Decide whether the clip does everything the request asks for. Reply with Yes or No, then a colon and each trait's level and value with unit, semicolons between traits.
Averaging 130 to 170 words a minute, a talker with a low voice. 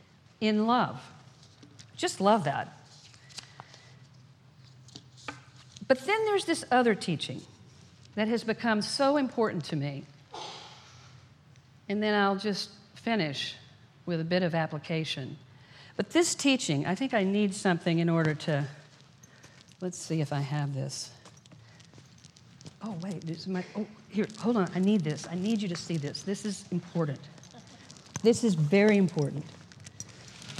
No: slow, 135 wpm; medium, 155 Hz